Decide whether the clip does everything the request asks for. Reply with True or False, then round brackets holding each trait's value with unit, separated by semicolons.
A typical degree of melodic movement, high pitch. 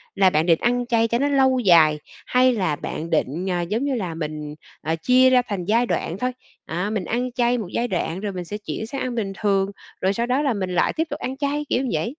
False (6.0 semitones; 210 Hz)